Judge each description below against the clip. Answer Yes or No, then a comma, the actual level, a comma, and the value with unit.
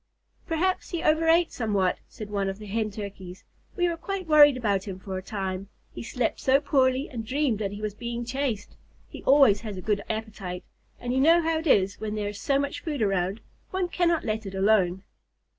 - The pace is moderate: No, fast, 210 wpm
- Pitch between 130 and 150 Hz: No, high, 220 Hz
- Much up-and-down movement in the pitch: Yes, wide, 6.5 semitones